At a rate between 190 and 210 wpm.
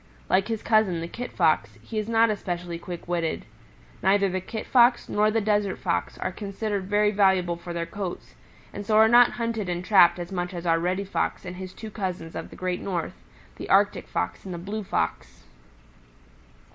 Yes: average, 195 wpm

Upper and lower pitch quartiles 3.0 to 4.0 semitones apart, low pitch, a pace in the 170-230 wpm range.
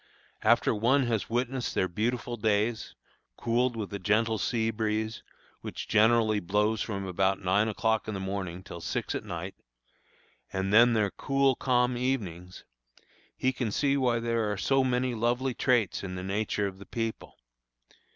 No: average, 3.3 semitones; low, 110 Hz; average, 160 wpm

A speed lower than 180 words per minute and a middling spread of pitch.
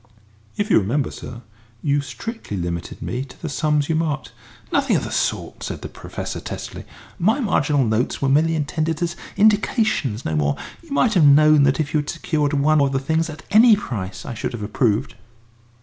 No: average, 195 wpm; average, 4.6 semitones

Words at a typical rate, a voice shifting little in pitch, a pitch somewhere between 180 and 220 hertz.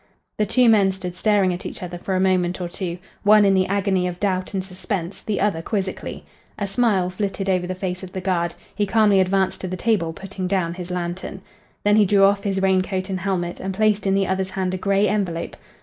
No: fast, 230 wpm; narrow, 1.6 semitones; high, 190 Hz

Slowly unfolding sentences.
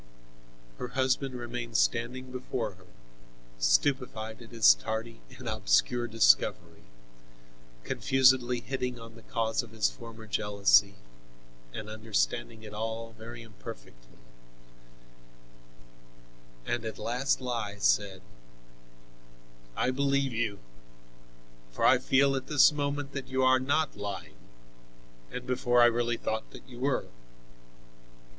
Yes: slow, 115 wpm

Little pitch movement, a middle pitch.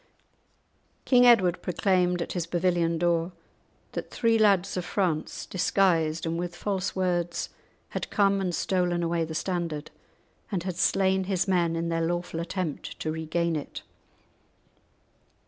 Yes: narrow, 2.1 semitones; medium, 175 Hz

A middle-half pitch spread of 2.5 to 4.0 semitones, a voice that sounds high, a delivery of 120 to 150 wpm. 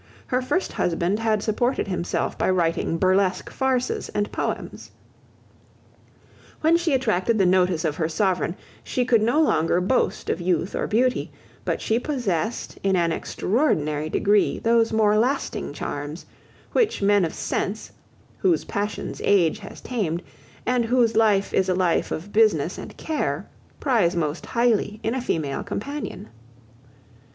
No: wide, 5.4 semitones; high, 205 Hz; average, 145 wpm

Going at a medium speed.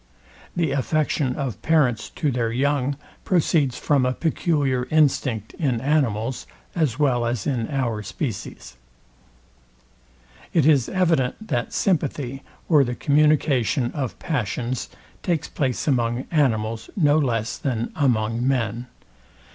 No: slow, 120 wpm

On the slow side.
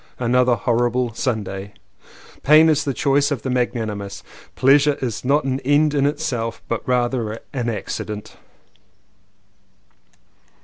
Yes: slow, 120 wpm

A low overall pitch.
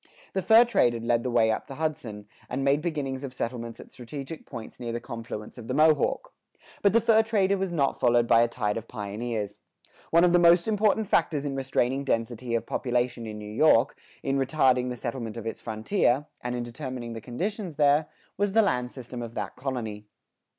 Yes: low, 125 Hz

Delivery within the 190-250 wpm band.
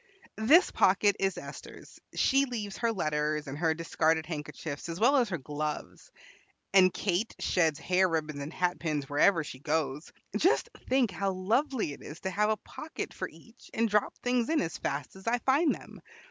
No: average, 180 wpm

